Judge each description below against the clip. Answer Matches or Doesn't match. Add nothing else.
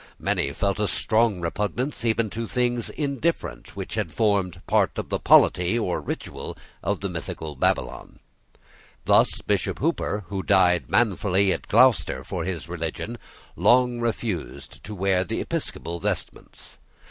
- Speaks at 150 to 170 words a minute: Doesn't match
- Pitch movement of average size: Matches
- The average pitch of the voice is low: Matches